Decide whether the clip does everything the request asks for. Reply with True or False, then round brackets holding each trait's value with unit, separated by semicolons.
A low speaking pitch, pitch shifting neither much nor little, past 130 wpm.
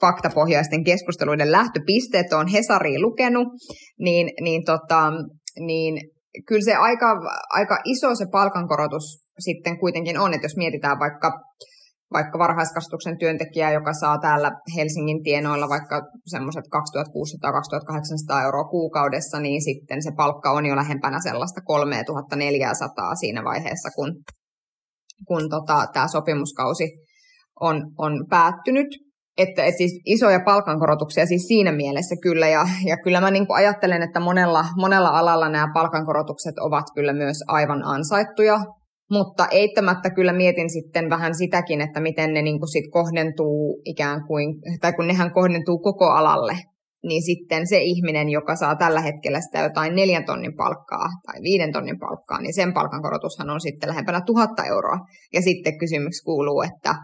False (165 Hz; 3.2 semitones; 140 wpm)